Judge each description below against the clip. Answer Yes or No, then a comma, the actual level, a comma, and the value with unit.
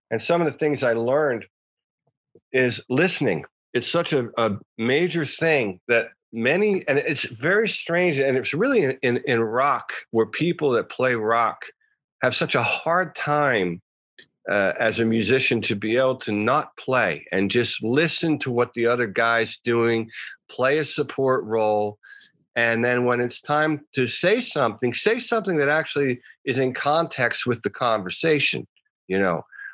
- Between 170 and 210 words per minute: No, average, 160 wpm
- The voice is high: No, low, 130 Hz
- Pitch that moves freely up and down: Yes, wide, 5.7 semitones